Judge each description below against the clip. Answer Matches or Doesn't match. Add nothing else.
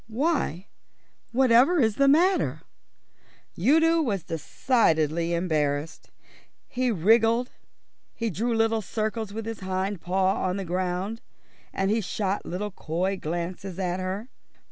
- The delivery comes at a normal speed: Doesn't match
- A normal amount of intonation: Matches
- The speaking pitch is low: Doesn't match